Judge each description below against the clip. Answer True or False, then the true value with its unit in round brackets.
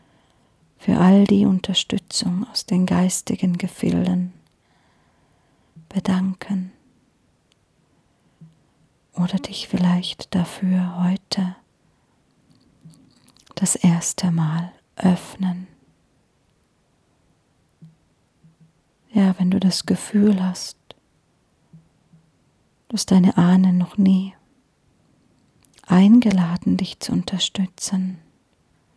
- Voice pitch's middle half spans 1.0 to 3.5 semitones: True (2.7 semitones)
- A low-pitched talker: False (185 Hz)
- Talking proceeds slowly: True (70 wpm)